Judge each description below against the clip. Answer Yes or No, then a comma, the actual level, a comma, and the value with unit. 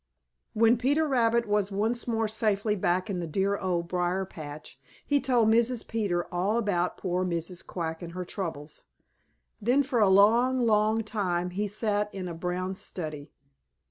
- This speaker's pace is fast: No, average, 165 wpm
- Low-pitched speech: No, high, 200 Hz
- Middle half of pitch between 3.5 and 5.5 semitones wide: Yes, average, 4.1 semitones